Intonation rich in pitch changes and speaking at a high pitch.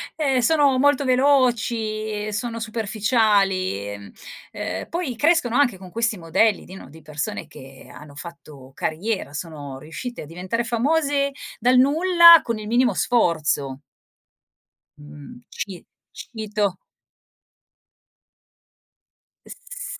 Yes: wide, 7.4 semitones; high, 220 Hz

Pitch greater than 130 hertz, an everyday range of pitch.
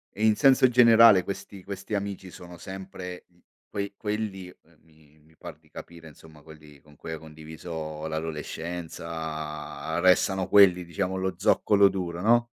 No: very low, 90 Hz; average, 3.8 semitones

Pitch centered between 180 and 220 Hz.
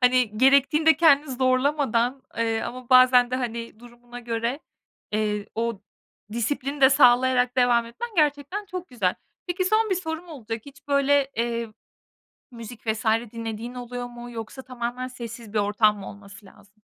No: high, 245 Hz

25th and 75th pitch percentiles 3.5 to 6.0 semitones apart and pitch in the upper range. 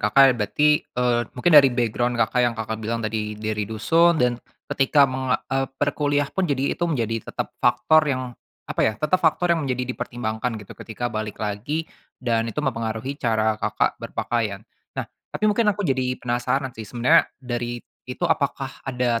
No: average, 4.0 semitones; low, 125 Hz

